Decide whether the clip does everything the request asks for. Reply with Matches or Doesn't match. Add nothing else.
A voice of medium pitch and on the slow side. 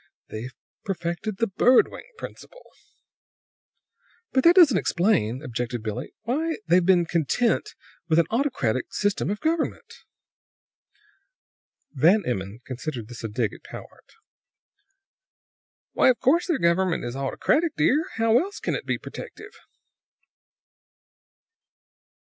Matches